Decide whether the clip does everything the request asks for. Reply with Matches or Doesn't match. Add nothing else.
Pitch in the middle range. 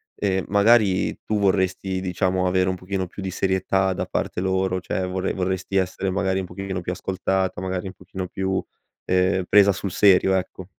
Doesn't match